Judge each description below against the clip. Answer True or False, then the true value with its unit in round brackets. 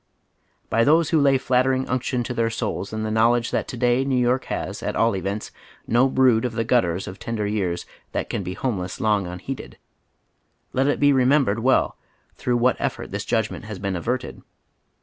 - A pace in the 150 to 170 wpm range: False (190 wpm)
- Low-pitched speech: True (120 Hz)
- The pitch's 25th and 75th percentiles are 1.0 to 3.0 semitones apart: False (3.4 semitones)